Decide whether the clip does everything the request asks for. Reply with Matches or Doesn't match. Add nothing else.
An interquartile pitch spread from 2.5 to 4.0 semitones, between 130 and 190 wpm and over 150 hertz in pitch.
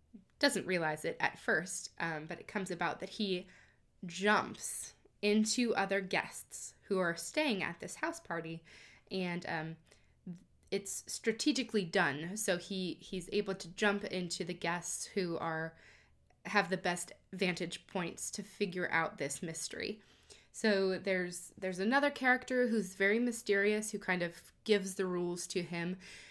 Matches